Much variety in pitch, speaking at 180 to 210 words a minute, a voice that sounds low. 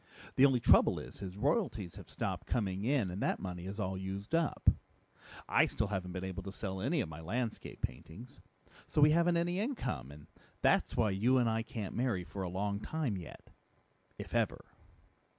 Yes: wide, 5.7 semitones; average, 190 wpm; low, 100 Hz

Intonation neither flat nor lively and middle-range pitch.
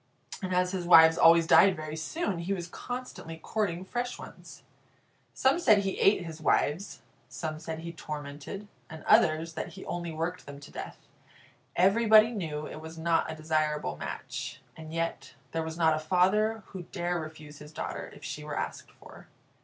Yes: average, 3.3 semitones; medium, 165 Hz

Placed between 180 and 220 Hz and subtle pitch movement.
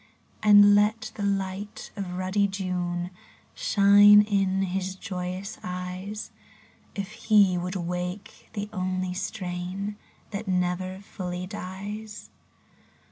Yes: high, 190 Hz; narrow, 2.0 semitones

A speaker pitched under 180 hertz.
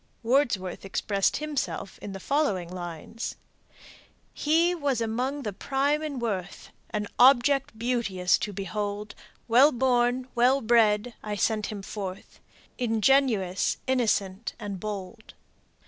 No: high, 225 Hz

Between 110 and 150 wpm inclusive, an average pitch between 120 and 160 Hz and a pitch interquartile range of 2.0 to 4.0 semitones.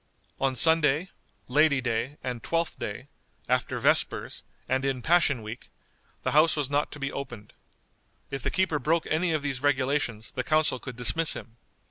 No: average, 165 wpm; medium, 140 Hz; average, 3.7 semitones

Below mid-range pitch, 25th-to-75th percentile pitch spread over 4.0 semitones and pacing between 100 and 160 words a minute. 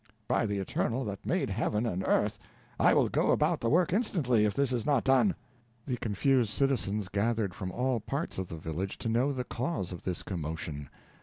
No: low, 115 Hz; wide, 5.6 semitones; average, 200 wpm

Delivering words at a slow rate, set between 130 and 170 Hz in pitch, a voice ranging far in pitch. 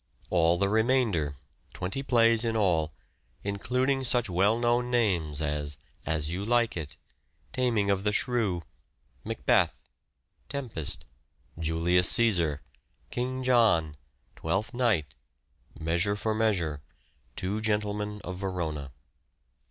No: slow, 110 wpm; low, 100 Hz; wide, 5.9 semitones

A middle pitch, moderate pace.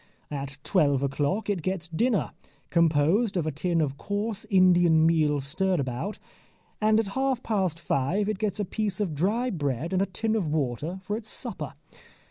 Yes: medium, 180 Hz; average, 170 wpm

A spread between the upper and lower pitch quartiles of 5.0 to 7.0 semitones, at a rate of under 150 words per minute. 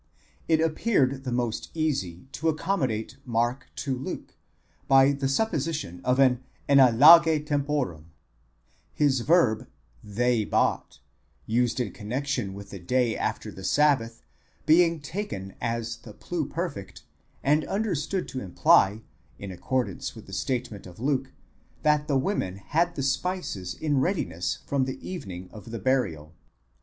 Yes: wide, 5.4 semitones; slow, 135 wpm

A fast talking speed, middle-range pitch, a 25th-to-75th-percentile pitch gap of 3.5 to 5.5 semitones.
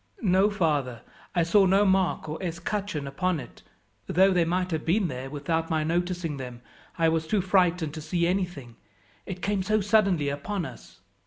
No: average, 175 wpm; medium, 170 Hz; average, 3.8 semitones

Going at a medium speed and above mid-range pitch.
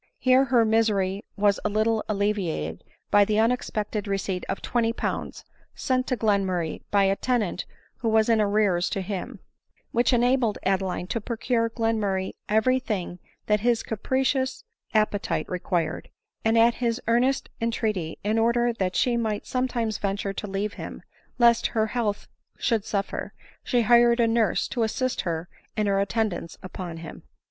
Yes: average, 155 wpm; high, 215 Hz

